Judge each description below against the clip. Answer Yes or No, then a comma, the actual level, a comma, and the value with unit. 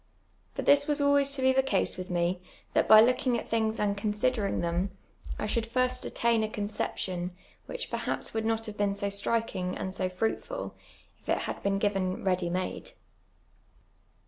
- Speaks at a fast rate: No, average, 175 wpm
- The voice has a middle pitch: No, high, 210 Hz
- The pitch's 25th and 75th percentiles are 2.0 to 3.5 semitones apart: No, average, 4.0 semitones